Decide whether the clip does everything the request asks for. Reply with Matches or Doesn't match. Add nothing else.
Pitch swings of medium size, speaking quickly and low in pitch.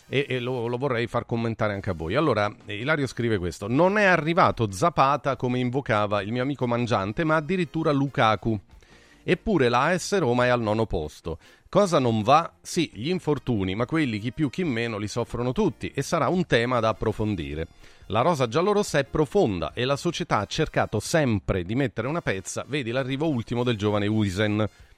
Doesn't match